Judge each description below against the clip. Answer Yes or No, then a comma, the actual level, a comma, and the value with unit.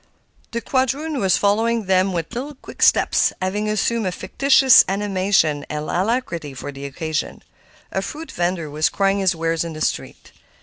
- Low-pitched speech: No, high, 190 Hz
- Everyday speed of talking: Yes, average, 165 wpm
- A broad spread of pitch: Yes, wide, 5.9 semitones